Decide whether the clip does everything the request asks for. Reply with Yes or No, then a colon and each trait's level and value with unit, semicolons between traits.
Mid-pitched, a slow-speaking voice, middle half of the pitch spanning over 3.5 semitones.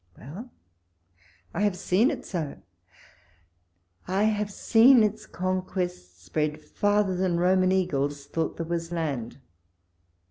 Yes: medium, 180 Hz; slow, 120 wpm; average, 4.7 semitones